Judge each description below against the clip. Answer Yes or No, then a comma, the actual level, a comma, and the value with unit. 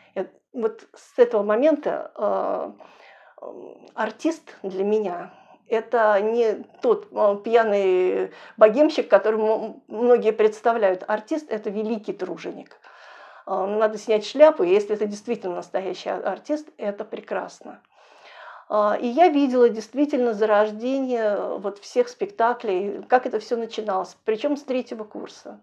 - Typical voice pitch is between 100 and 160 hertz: No, high, 220 Hz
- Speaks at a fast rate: No, slow, 110 wpm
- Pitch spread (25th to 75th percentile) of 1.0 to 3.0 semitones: No, average, 4.2 semitones